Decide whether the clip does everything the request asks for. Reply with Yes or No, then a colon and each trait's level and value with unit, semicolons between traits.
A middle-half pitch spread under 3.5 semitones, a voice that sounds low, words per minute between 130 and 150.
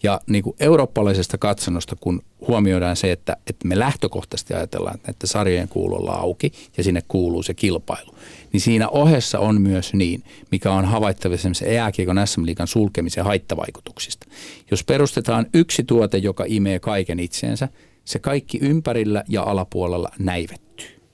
No: average, 4.0 semitones; low, 100 Hz; average, 145 wpm